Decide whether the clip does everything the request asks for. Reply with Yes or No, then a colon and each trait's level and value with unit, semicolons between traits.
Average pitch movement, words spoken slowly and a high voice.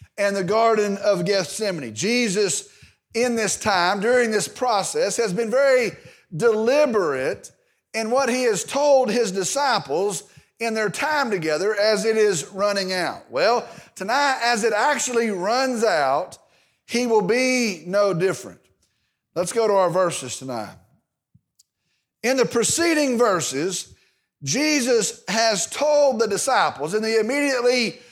Yes: average, 3.8 semitones; slow, 130 wpm; high, 225 Hz